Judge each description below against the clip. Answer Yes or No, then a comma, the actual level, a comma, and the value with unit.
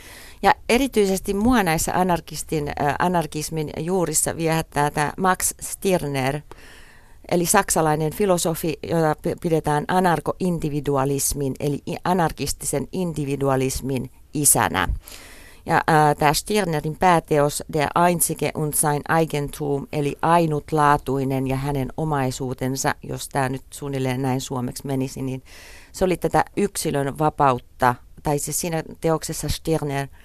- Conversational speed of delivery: Yes, average, 110 wpm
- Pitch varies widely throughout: No, average, 3.0 semitones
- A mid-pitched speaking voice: Yes, medium, 150 Hz